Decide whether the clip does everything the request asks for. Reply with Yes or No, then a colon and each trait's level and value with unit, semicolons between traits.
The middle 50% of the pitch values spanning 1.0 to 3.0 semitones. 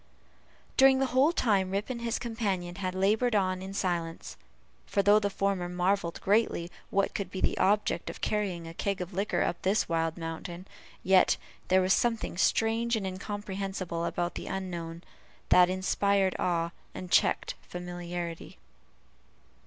Yes: average, 2.7 semitones